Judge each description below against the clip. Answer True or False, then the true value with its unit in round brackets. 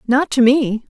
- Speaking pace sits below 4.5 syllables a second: True (4.0 syllables/s)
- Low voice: False (255 Hz)